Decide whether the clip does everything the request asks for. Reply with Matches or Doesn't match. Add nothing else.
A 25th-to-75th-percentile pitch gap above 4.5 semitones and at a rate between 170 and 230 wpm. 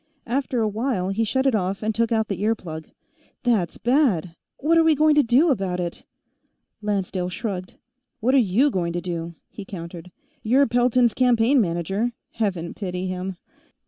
Matches